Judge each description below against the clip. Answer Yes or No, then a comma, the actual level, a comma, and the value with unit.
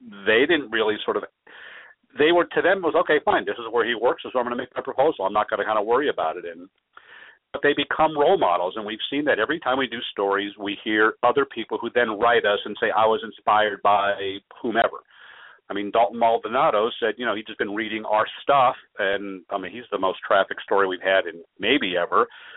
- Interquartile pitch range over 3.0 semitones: Yes, average, 3.4 semitones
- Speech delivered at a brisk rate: Yes, fast, 235 wpm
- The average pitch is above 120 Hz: No, low, 110 Hz